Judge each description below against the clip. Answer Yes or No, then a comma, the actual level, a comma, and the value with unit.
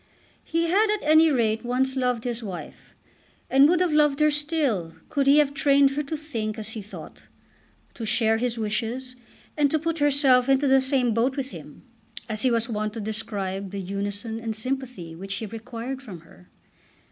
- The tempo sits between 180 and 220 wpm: Yes, average, 190 wpm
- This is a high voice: Yes, very high, 250 Hz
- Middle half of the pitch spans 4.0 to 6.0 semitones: Yes, average, 4.5 semitones